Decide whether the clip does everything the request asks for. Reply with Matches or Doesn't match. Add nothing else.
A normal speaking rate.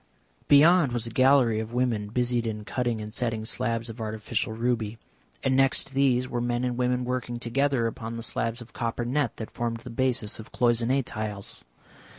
Matches